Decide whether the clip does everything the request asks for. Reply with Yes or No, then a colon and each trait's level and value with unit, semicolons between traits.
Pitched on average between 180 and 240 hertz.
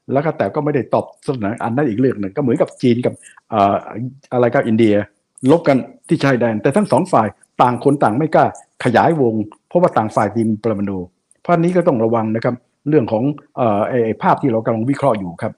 No: low, 120 Hz